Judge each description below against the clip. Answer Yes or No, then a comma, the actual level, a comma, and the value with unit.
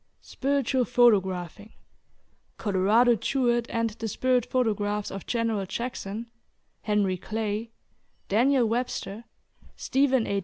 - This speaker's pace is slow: Yes, slow, 100 wpm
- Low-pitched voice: No, high, 225 Hz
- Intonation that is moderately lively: Yes, average, 3.1 semitones